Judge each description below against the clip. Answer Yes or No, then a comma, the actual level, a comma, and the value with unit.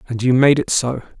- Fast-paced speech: Yes, fast, 250 wpm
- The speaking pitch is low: Yes, low, 125 Hz